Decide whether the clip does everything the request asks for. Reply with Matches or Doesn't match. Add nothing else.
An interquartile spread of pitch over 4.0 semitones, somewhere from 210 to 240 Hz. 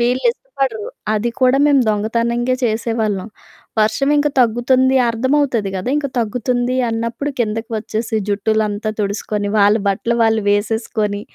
Doesn't match